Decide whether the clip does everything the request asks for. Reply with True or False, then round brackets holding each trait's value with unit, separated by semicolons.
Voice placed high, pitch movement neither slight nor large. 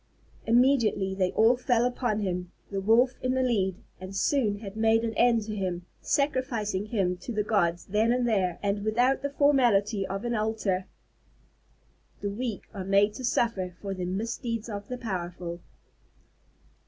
True (215 Hz; 3.8 semitones)